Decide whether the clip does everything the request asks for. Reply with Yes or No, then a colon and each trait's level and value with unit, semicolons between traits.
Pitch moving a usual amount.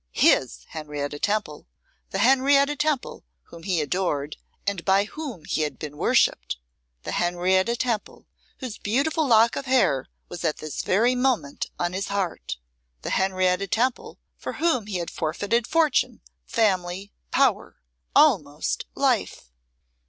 No: wide, 6.4 semitones